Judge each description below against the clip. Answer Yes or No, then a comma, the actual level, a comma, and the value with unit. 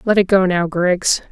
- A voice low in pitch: No, medium, 185 Hz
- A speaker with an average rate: No, fast, 230 wpm